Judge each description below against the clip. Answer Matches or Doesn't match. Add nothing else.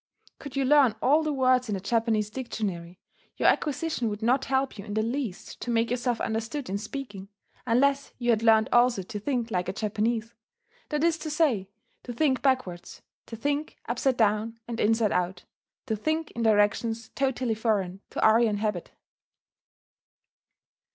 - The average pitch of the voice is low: Doesn't match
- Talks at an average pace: Matches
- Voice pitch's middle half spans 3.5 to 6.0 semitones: Matches